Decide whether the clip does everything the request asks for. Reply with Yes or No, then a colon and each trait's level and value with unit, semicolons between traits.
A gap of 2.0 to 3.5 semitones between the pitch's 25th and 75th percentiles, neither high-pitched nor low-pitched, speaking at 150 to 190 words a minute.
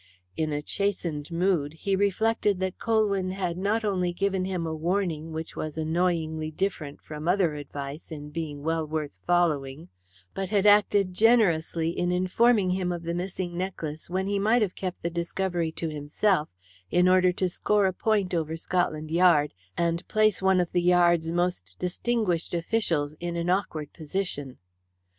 Yes: average, 3.2 semitones; medium, 175 Hz; average, 165 wpm